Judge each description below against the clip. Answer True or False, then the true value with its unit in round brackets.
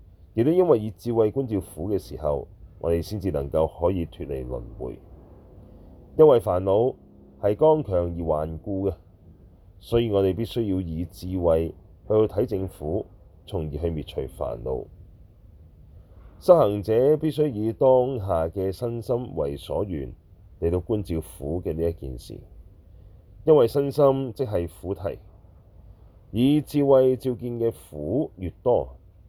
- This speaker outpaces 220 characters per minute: False (200 characters per minute)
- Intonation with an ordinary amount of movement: True (4.8 semitones)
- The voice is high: False (95 Hz)